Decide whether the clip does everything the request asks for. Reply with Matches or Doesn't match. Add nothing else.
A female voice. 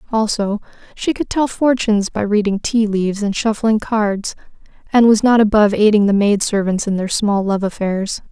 Matches